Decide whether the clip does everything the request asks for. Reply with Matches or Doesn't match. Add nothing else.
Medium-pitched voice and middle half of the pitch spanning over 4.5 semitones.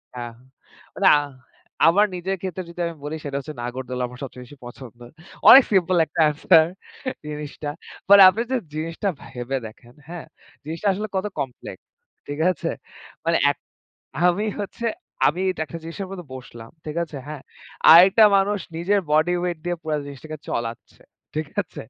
Matches